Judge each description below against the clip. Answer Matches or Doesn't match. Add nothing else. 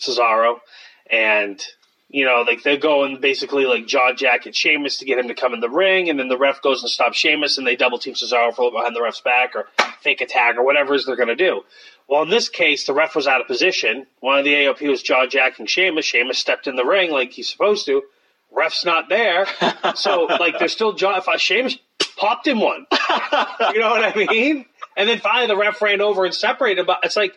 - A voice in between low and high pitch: Matches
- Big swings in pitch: Matches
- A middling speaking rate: Doesn't match